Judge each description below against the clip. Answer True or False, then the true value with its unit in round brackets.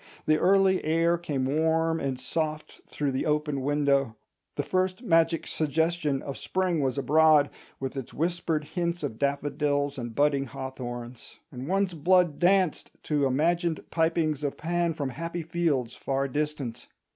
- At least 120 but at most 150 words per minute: True (145 wpm)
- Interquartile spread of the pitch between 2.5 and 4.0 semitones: True (3.4 semitones)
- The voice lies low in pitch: False (150 Hz)